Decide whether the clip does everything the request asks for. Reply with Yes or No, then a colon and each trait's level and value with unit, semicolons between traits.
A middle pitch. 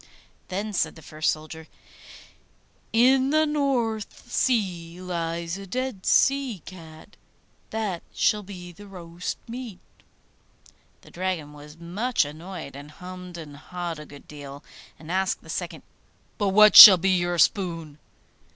Yes: medium, 180 Hz